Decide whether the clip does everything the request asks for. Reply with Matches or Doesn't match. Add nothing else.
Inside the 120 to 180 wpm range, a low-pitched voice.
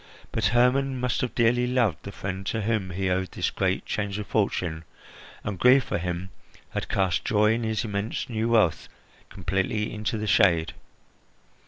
Matches